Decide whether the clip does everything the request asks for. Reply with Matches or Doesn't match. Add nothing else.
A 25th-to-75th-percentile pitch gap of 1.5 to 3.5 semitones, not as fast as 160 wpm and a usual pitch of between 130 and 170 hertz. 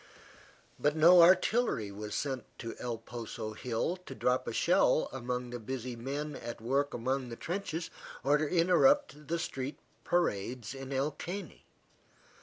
Doesn't match